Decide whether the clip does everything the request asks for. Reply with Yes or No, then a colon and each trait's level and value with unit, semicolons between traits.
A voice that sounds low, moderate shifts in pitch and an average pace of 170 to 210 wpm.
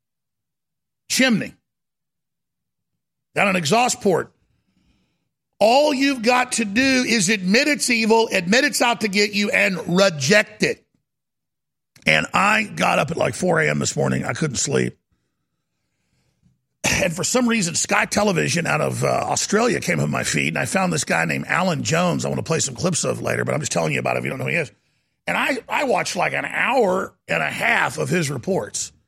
No: high, 220 Hz; average, 3.9 semitones; average, 190 wpm